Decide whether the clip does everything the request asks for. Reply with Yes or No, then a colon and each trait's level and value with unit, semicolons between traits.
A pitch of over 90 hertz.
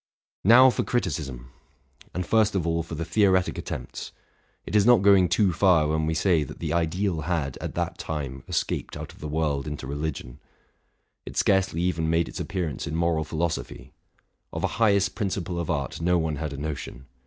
No: very low, 85 Hz